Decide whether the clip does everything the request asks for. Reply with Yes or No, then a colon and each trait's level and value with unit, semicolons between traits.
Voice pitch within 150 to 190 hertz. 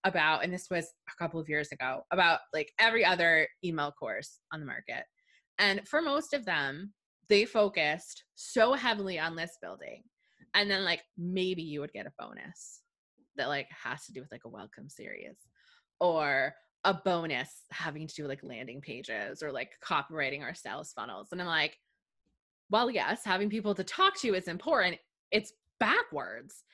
Yes: medium, 185 Hz